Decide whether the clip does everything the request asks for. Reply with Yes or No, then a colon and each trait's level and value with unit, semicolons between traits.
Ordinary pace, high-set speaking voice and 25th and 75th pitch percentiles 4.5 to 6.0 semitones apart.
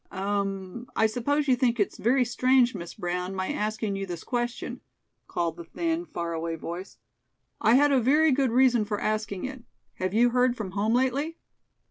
Yes: average, 180 wpm; high, 225 Hz; average, 4.9 semitones